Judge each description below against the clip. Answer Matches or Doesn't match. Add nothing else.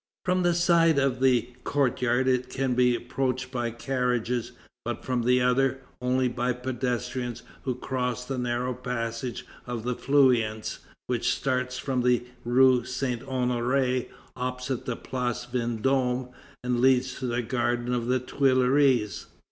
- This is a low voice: Matches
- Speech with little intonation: Matches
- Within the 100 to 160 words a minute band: Matches